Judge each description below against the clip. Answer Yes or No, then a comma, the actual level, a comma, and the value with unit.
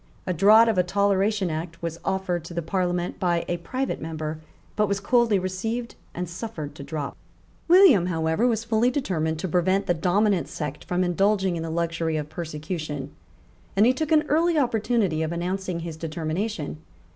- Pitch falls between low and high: Yes, medium, 180 Hz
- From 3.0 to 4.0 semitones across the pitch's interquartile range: No, average, 4.6 semitones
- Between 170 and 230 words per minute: Yes, average, 175 wpm